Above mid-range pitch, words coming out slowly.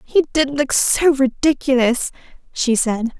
Yes: very high, 265 Hz; slow, 130 wpm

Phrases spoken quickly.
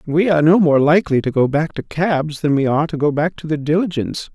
Yes: fast, 265 wpm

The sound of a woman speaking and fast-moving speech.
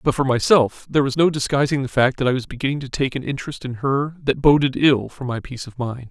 No: male; fast, 265 wpm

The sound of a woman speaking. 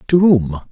No: male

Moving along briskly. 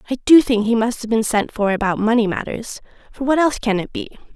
Yes: fast, 250 wpm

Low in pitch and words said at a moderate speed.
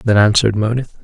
Yes: low, 110 Hz; average, 175 wpm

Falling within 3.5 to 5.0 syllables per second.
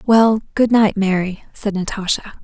Yes: 4.5 syllables/s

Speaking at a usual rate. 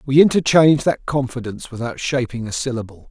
Yes: average, 155 wpm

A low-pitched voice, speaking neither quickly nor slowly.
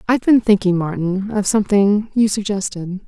No: high, 200 Hz; average, 155 wpm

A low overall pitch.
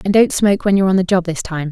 No: medium, 185 Hz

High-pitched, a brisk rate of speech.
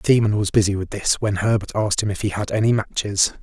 No: low, 105 Hz; fast, 260 wpm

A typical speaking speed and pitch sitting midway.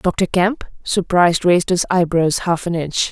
Yes: average, 175 wpm; medium, 175 Hz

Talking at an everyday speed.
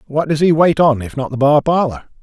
No: fast, 270 wpm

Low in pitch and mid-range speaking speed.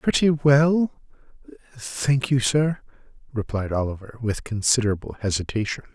No: low, 125 Hz; slow, 100 wpm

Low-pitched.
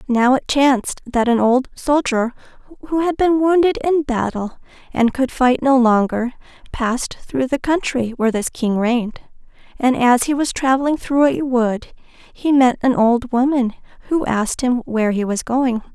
No: very high, 255 Hz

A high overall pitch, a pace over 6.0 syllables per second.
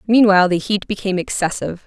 Yes: high, 195 Hz; 7.0 syllables/s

